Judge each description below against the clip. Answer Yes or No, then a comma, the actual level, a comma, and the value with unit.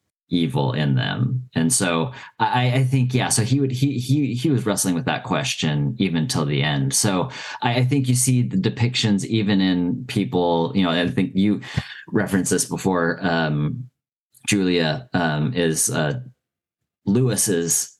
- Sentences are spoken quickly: No, average, 165 wpm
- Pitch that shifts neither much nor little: No, wide, 6.9 semitones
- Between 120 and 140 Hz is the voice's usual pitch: No, low, 100 Hz